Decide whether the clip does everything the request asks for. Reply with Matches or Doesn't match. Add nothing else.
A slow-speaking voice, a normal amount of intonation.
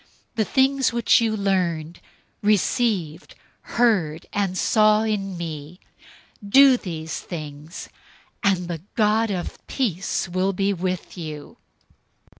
Matches